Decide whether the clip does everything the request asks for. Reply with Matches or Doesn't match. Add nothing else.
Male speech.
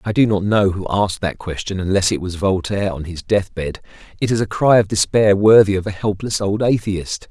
Matches